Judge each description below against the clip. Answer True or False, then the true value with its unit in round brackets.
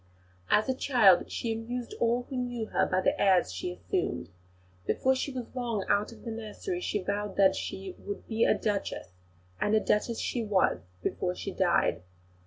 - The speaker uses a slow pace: False (185 wpm)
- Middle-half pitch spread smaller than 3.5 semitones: False (3.9 semitones)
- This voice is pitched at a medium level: False (220 Hz)